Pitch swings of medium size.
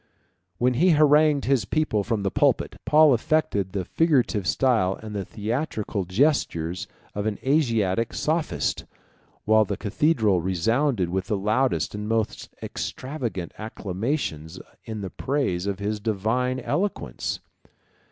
No: wide, 5.8 semitones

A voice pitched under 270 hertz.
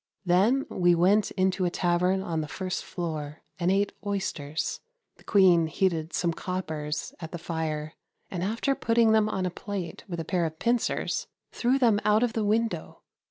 Yes: medium, 185 Hz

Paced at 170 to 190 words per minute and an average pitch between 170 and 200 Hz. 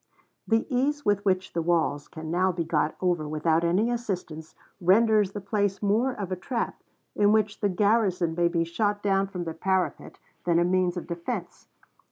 Yes: average, 185 wpm; medium, 185 Hz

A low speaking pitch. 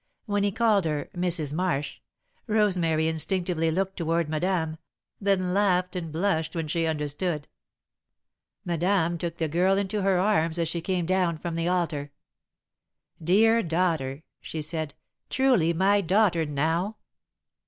No: medium, 170 Hz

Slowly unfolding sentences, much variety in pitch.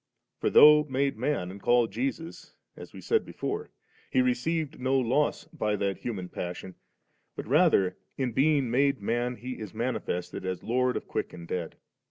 No: average, 175 wpm; wide, 5.9 semitones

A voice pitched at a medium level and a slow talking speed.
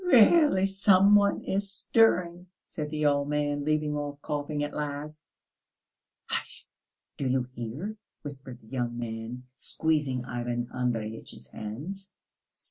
Yes: medium, 145 Hz; slow, 125 wpm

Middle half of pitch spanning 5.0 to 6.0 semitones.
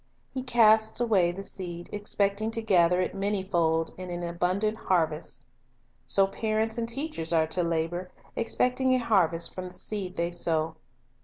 No: average, 4.2 semitones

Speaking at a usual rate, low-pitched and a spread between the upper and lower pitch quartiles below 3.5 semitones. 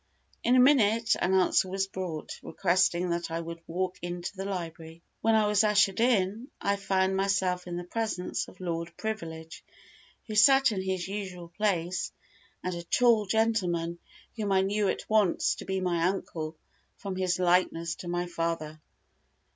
No: average, 165 wpm; medium, 185 Hz; average, 3.1 semitones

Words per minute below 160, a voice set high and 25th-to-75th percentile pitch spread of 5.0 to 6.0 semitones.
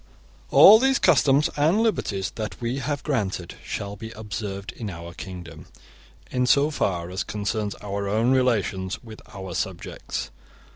No: average, 150 wpm; low, 105 Hz; wide, 5.5 semitones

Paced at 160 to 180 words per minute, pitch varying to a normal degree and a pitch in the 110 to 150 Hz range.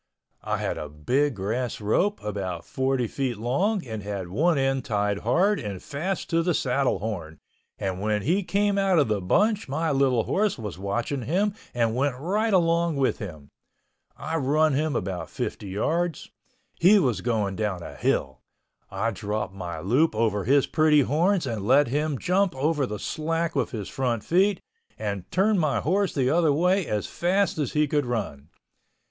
No: average, 175 wpm; wide, 8.0 semitones; low, 135 Hz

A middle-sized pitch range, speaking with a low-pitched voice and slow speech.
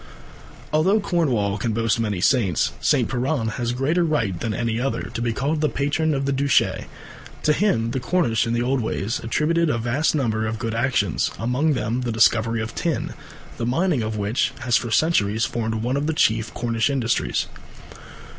No: average, 4.3 semitones; low, 120 Hz; average, 185 wpm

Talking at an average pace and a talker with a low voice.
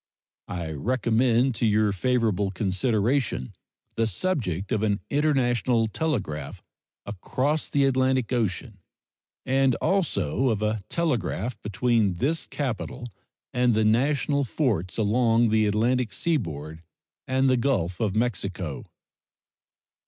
No: slow, 110 wpm; low, 115 Hz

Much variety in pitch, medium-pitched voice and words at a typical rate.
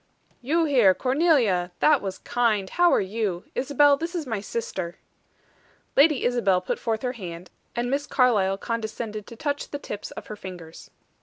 No: wide, 6.5 semitones; high, 230 Hz; average, 165 wpm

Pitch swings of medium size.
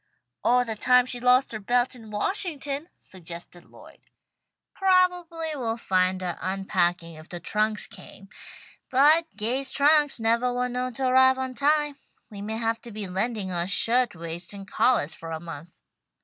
No: wide, 5.7 semitones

